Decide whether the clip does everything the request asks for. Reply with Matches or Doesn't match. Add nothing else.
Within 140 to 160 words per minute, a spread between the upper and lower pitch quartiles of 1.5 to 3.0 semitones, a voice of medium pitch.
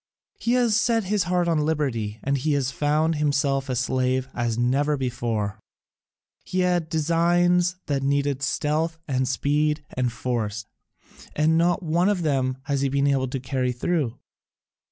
Doesn't match